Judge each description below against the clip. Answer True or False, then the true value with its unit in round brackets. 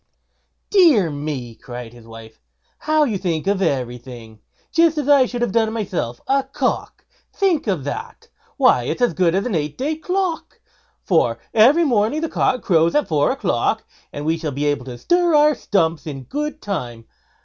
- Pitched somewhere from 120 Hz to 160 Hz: False (190 Hz)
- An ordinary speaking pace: True (180 wpm)